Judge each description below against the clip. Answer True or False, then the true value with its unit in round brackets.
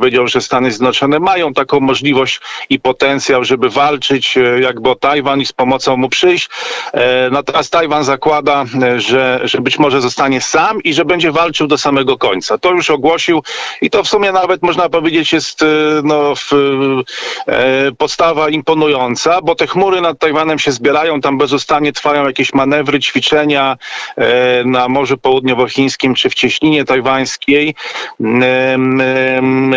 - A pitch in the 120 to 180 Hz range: True (140 Hz)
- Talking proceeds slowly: False (155 wpm)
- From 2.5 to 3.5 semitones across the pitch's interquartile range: True (3.0 semitones)